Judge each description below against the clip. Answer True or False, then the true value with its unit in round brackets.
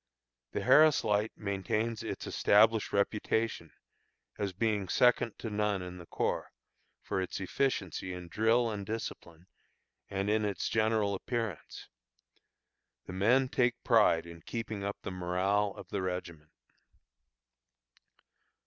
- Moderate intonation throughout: True (3.3 semitones)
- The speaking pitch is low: True (105 Hz)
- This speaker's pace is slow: True (125 wpm)